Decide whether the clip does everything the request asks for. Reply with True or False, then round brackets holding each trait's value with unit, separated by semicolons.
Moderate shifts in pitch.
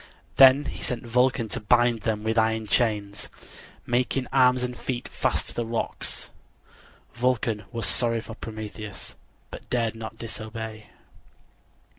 False (2.0 semitones)